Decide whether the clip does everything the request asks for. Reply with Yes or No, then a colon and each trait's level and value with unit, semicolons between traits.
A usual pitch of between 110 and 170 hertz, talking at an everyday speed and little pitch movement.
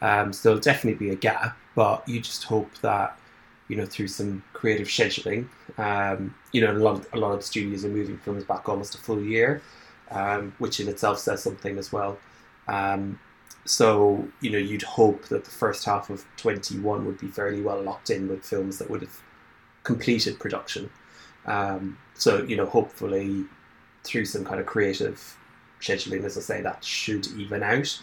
No: low, 100 Hz; average, 185 wpm; narrow, 1.6 semitones